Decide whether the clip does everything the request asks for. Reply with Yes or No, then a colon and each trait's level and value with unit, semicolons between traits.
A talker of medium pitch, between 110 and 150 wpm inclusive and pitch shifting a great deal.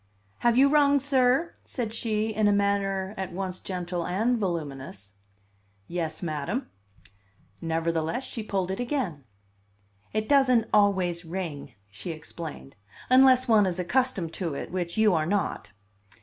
No: high, 195 Hz; slow, 135 wpm; wide, 5.8 semitones